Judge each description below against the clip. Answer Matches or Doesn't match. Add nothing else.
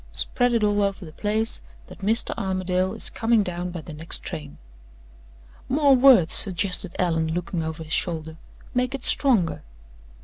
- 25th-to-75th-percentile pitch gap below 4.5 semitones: Doesn't match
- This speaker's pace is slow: Doesn't match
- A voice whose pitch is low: Doesn't match